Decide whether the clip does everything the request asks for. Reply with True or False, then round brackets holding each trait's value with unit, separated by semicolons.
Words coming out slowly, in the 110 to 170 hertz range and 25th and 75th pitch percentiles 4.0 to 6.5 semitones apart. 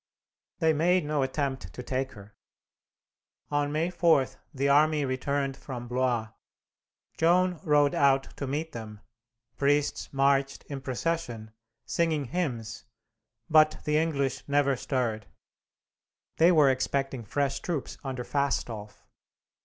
False (120 wpm; 140 Hz; 2.9 semitones)